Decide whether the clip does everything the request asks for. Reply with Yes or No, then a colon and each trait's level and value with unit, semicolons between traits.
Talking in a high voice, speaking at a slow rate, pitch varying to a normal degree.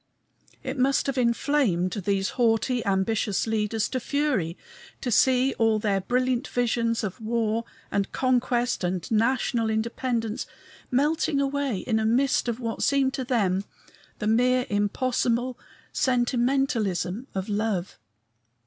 Yes: high, 235 Hz; slow, 125 wpm; average, 3.4 semitones